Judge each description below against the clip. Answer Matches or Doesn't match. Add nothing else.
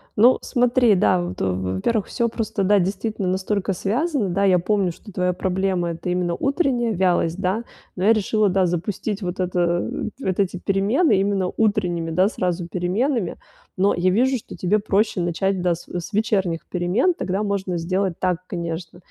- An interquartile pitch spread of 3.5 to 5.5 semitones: Doesn't match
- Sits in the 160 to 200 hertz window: Matches